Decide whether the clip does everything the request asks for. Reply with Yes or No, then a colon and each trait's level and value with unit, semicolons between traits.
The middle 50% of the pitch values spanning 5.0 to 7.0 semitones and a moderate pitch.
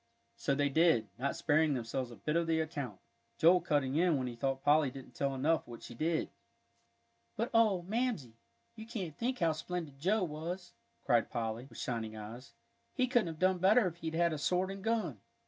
Yes: wide, 5.4 semitones; medium, 160 Hz